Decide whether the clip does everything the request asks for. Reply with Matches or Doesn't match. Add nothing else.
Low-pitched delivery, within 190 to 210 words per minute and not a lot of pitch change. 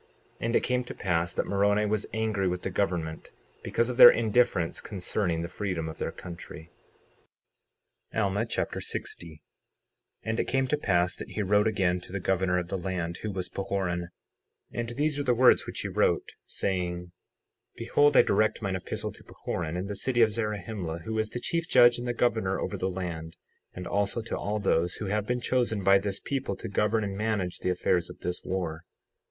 Doesn't match